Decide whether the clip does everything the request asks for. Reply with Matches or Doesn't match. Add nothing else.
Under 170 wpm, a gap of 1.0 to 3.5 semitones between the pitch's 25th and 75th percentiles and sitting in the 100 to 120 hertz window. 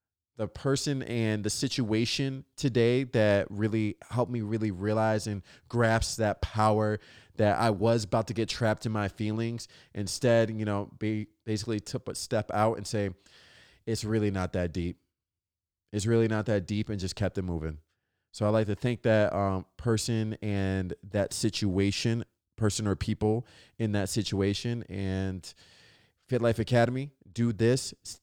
Matches